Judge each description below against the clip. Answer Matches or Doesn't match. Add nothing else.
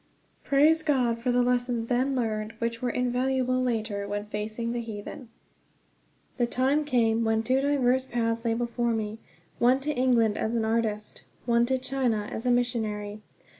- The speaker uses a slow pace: Doesn't match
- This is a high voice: Matches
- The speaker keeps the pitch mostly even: Matches